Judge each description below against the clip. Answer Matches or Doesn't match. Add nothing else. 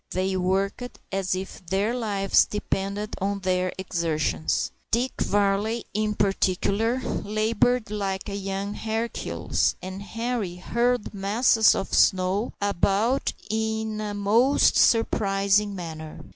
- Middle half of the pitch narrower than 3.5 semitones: Matches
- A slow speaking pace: Matches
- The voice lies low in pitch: Doesn't match